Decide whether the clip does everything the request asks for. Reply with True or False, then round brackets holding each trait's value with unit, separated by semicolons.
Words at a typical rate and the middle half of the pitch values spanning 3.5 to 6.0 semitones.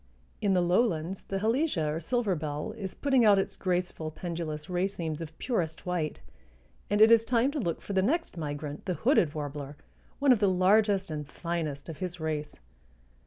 True (180 wpm; 5.0 semitones)